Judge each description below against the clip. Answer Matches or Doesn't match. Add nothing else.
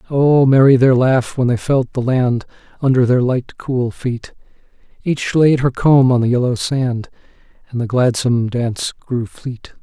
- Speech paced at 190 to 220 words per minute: Doesn't match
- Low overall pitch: Matches